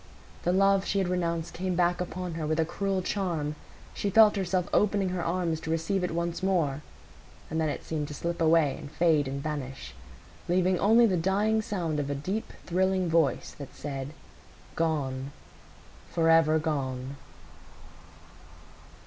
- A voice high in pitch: No, medium, 170 Hz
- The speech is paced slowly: No, average, 155 wpm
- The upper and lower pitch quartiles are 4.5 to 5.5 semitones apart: No, average, 3.5 semitones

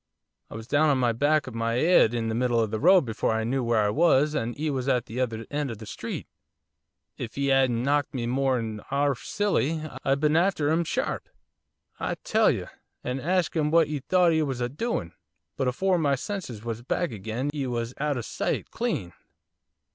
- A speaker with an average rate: No, fast, 215 wpm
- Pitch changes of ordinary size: Yes, average, 4.7 semitones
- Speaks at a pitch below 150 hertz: Yes, low, 135 Hz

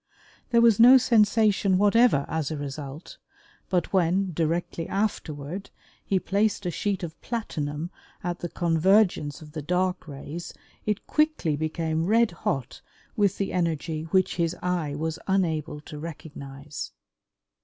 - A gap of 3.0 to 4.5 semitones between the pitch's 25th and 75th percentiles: Yes, average, 4.2 semitones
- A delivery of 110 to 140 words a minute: Yes, slow, 135 wpm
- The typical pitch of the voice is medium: Yes, medium, 170 Hz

